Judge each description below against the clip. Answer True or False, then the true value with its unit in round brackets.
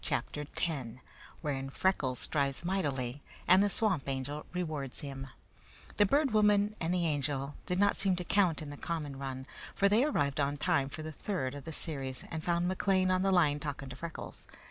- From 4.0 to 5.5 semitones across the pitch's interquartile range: True (5.1 semitones)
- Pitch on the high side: False (155 Hz)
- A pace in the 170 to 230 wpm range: True (190 wpm)